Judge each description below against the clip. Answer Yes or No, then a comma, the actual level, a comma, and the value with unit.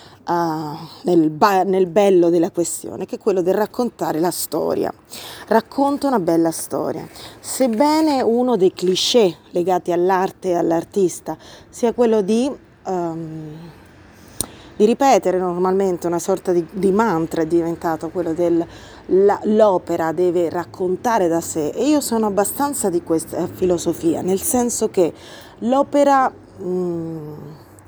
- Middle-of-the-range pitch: Yes, medium, 180 Hz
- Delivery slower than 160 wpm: Yes, average, 125 wpm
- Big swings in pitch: No, average, 4.6 semitones